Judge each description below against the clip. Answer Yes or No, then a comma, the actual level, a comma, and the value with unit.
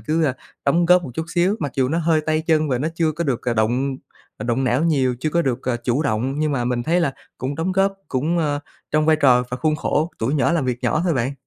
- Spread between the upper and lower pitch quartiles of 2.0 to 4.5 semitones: Yes, average, 4.2 semitones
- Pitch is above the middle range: No, medium, 145 Hz